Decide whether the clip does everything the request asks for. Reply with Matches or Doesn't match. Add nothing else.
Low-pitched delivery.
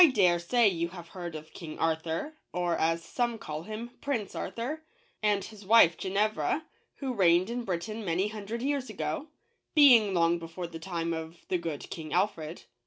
Doesn't match